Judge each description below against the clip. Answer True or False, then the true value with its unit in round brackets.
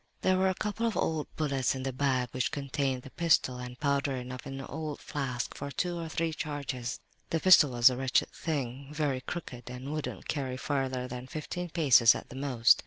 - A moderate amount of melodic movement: True (3.3 semitones)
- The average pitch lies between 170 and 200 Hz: False (135 Hz)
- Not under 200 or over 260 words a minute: True (205 wpm)